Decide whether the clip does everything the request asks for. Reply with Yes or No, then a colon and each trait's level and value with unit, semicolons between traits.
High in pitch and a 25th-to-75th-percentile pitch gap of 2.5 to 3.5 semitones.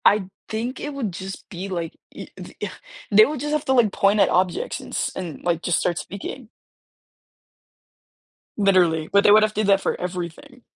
No: high, 200 Hz; average, 4.3 semitones